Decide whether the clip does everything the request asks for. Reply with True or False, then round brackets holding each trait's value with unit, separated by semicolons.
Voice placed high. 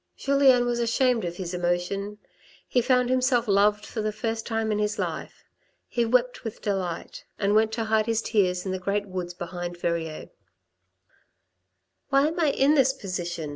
True (210 Hz)